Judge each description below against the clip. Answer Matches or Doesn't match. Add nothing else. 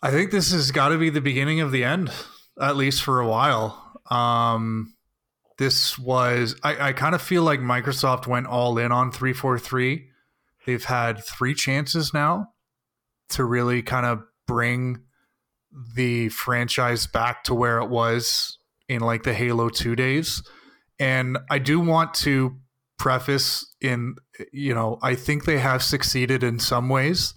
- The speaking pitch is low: Matches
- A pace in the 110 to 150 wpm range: Doesn't match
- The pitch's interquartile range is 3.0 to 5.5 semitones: Doesn't match